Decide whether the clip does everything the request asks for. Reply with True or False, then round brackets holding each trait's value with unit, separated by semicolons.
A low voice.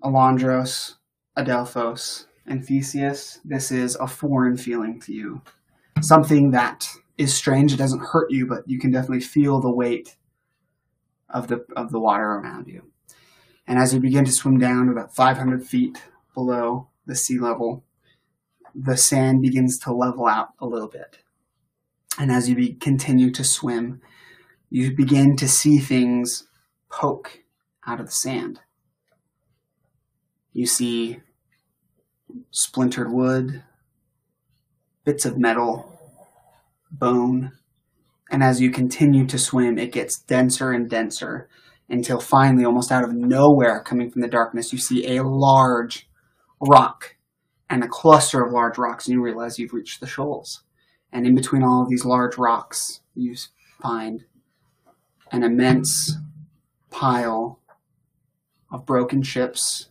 True (125 Hz)